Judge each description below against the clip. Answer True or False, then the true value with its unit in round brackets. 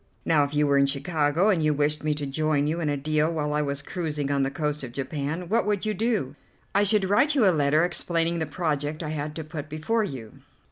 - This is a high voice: False (155 Hz)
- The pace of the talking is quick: True (245 wpm)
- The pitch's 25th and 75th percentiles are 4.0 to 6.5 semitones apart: False (2.9 semitones)